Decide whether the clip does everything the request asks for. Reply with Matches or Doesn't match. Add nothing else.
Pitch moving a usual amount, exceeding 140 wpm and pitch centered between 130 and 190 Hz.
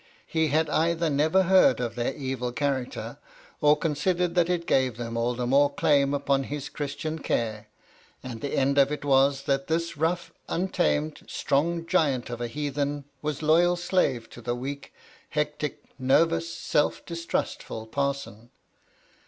Matches